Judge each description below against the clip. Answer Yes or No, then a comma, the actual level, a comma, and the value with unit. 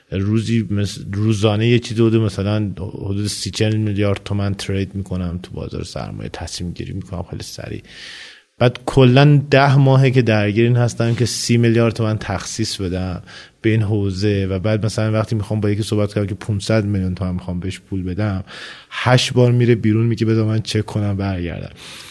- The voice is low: Yes, low, 105 Hz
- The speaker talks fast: Yes, fast, 175 wpm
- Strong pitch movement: No, average, 2.8 semitones